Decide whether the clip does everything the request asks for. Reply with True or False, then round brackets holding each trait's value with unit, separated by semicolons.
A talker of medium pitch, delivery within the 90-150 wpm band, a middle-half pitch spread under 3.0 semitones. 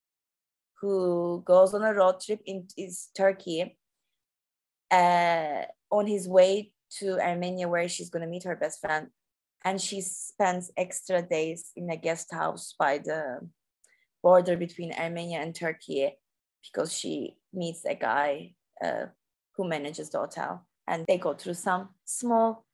True (180 Hz; 140 wpm; 2.4 semitones)